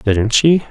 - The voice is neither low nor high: No, low, 125 Hz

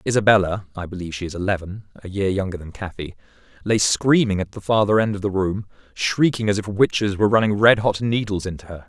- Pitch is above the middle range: No, low, 100 Hz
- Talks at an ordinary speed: Yes, average, 195 wpm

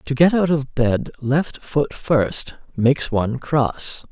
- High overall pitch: No, low, 135 Hz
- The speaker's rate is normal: Yes, average, 160 wpm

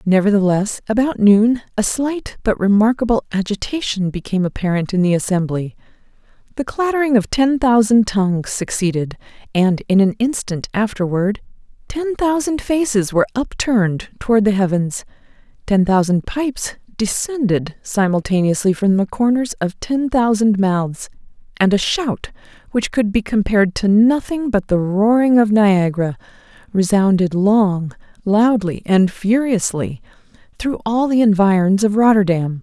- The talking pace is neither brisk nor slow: No, slow, 130 wpm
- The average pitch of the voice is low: No, high, 210 Hz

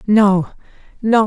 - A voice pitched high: Yes, high, 210 Hz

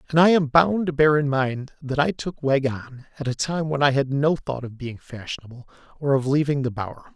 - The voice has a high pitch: No, medium, 140 Hz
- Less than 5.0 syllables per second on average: No, 5.3 syllables/s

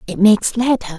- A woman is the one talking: No, male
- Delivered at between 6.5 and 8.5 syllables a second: No, 6.0 syllables/s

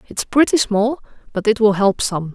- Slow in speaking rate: No, fast, 205 wpm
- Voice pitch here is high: Yes, high, 215 Hz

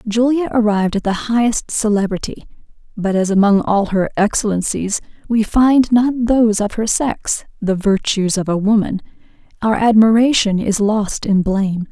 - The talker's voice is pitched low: No, high, 215 Hz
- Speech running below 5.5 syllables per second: Yes, 4.7 syllables/s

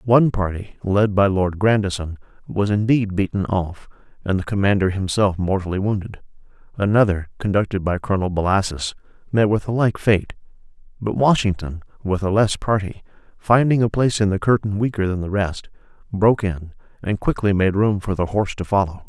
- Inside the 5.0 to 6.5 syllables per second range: Yes, 5.5 syllables/s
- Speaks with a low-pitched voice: Yes, low, 100 Hz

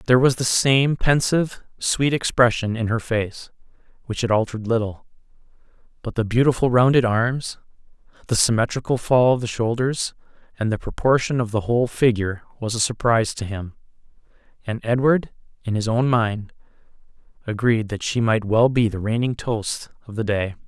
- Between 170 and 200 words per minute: No, average, 160 wpm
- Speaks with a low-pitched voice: Yes, low, 115 Hz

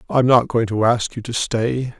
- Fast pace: Yes, fast, 240 wpm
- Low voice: Yes, low, 120 Hz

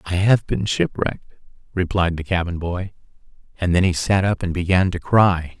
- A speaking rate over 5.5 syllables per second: No, 5.1 syllables/s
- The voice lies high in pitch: No, very low, 90 Hz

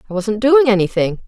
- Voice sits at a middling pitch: No, high, 225 Hz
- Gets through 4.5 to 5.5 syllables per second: No, 5.8 syllables/s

